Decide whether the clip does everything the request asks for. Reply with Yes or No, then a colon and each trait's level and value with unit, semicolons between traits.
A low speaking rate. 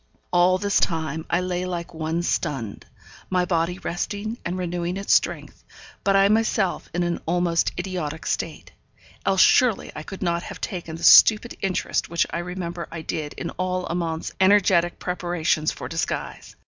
No: average, 160 wpm